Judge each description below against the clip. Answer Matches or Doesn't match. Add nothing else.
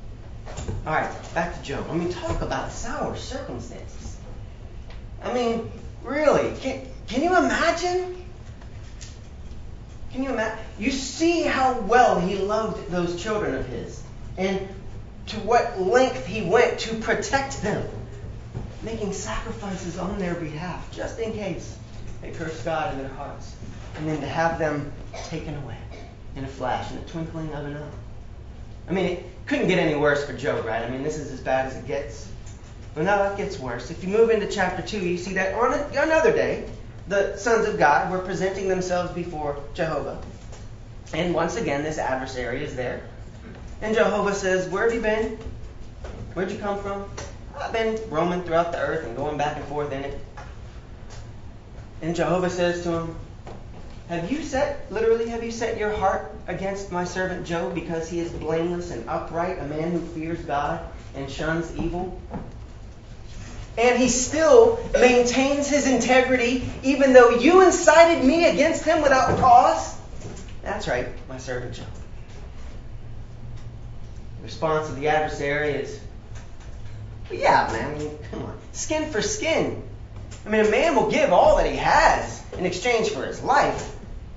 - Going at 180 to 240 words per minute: Doesn't match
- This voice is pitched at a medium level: Matches